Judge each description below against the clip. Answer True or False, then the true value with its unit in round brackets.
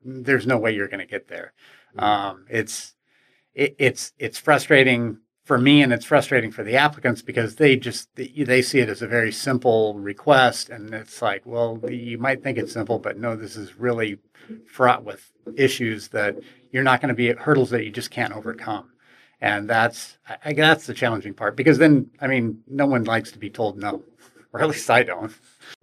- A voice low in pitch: True (120 Hz)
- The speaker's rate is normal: True (195 wpm)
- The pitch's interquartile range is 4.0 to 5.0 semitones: False (3.0 semitones)